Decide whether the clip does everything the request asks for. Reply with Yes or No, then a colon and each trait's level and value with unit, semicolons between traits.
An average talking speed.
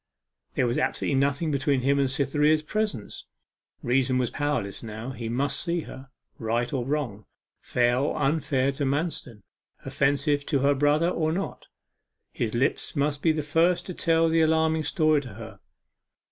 Yes: average, 160 wpm